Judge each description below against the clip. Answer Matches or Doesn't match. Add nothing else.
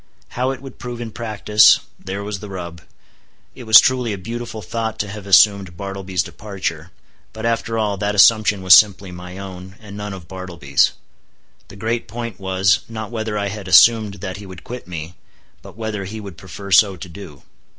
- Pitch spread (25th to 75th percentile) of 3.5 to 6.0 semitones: Doesn't match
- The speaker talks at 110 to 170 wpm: Doesn't match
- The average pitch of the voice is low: Matches